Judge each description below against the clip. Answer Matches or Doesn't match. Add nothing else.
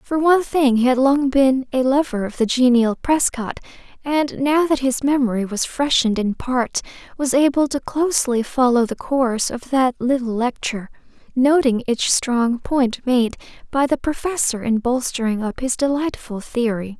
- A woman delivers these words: Matches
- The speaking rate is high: Doesn't match